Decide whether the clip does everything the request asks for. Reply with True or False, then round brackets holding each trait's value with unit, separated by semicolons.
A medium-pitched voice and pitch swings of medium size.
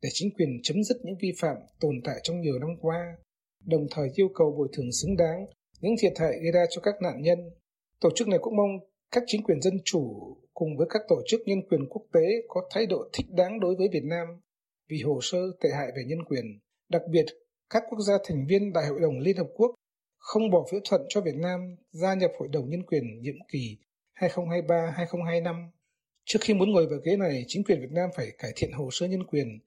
True (175 Hz; 3.7 semitones)